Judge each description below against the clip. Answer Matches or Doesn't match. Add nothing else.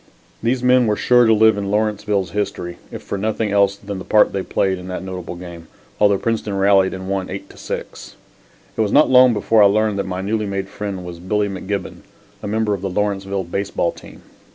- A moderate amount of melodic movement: Doesn't match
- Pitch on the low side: Matches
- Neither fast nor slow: Doesn't match